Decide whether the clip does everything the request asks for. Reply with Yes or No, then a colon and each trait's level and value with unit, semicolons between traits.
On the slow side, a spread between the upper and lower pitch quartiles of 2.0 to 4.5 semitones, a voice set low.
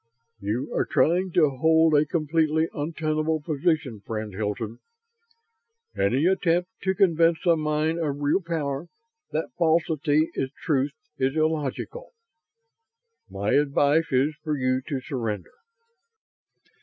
No: slow, 120 wpm; average, 3.4 semitones; medium, 155 Hz